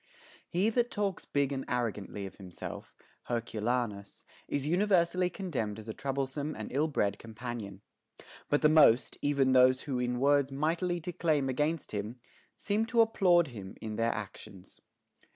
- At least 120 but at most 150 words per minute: No, average, 160 wpm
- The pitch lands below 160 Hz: Yes, low, 135 Hz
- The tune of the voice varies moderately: No, wide, 6.6 semitones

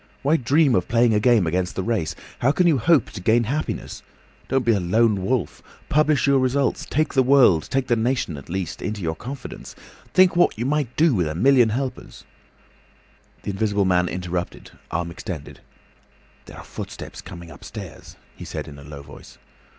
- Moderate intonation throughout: No, wide, 6.9 semitones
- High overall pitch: No, low, 115 Hz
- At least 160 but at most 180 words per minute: Yes, average, 175 wpm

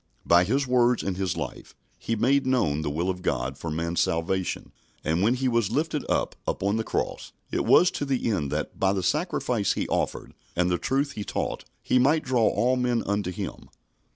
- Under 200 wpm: No, fast, 205 wpm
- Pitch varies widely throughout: Yes, wide, 6.3 semitones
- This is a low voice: Yes, low, 110 Hz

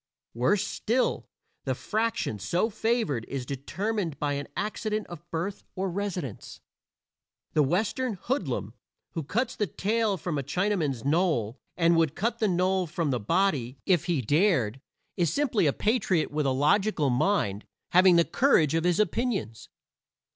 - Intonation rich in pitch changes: Yes, wide, 6.5 semitones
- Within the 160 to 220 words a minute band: No, average, 150 wpm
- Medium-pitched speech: Yes, medium, 175 Hz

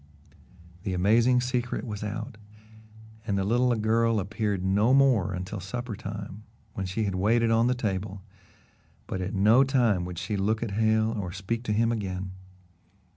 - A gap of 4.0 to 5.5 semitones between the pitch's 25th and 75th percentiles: No, average, 3.1 semitones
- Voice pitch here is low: Yes, low, 105 Hz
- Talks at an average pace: Yes, average, 160 wpm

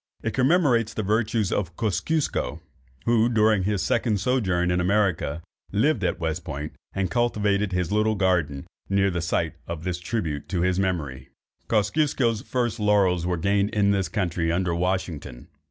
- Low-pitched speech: Yes, very low, 95 Hz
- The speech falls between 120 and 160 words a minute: Yes, average, 155 wpm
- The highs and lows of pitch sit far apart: No, average, 4.0 semitones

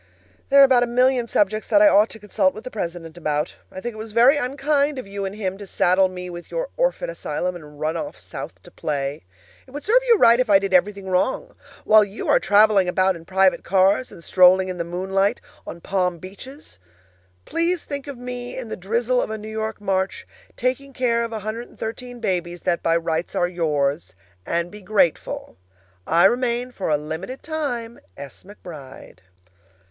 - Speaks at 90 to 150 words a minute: No, average, 195 wpm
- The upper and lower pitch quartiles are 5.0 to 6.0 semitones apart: Yes, wide, 5.6 semitones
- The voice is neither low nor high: No, high, 205 Hz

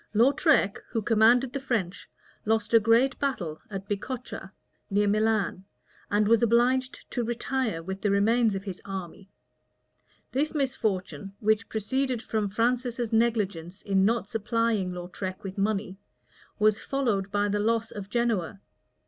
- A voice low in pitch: No, high, 215 Hz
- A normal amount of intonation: Yes, average, 3.3 semitones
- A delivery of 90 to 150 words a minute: Yes, average, 140 wpm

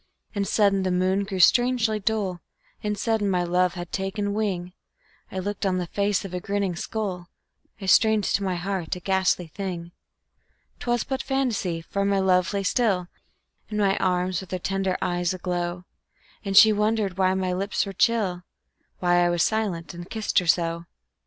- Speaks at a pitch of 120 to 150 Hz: No, high, 190 Hz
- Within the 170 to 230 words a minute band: Yes, average, 180 wpm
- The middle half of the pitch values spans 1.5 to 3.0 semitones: Yes, narrow, 2.5 semitones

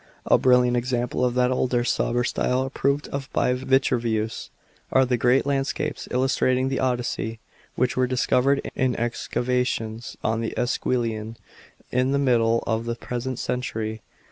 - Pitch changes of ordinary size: No, narrow, 1.8 semitones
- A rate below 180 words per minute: Yes, average, 145 wpm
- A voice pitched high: No, low, 125 Hz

